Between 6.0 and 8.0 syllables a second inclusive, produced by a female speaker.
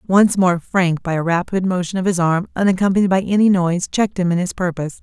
Yes: 6.1 syllables/s; female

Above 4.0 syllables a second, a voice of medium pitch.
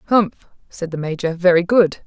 Yes: 5.4 syllables/s; medium, 180 Hz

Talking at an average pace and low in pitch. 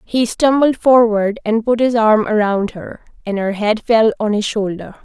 No: average, 190 wpm; high, 220 Hz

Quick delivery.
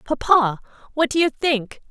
No: average, 155 wpm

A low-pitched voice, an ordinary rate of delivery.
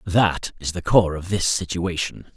Yes: very low, 90 Hz; average, 180 wpm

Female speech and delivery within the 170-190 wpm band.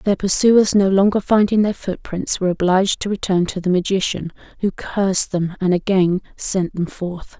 Yes: female; average, 180 wpm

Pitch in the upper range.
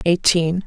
No: medium, 170 Hz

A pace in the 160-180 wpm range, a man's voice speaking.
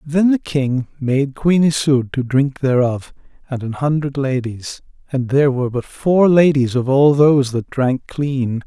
Yes: average, 175 wpm; male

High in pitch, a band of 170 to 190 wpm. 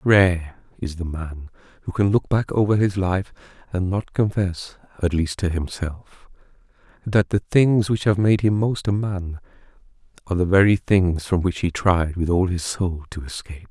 No: very low, 95 Hz; average, 185 wpm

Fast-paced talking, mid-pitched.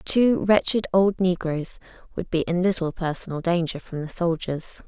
No: average, 160 wpm; medium, 180 Hz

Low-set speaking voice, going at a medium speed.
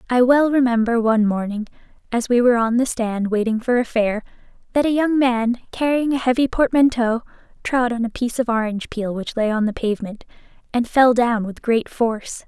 No: high, 235 Hz; average, 195 wpm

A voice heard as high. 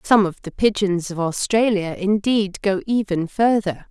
Yes: high, 195 Hz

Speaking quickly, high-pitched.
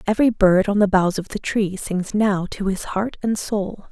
Yes: fast, 230 wpm; high, 200 Hz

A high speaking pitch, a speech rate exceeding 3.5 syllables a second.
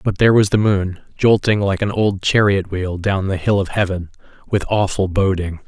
No: low, 100 Hz; 5.0 syllables/s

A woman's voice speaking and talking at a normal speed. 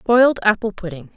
Yes: female; average, 155 wpm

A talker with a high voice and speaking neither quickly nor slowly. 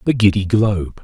No: low, 100 Hz; average, 175 wpm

